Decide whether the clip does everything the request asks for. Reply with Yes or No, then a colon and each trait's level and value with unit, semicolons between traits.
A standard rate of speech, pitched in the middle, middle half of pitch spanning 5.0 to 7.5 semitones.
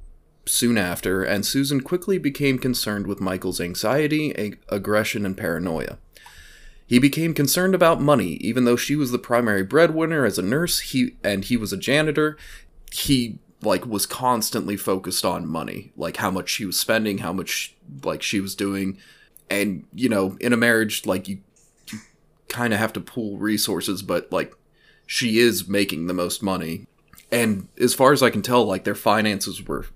No: average, 175 wpm; low, 110 Hz; average, 5.3 semitones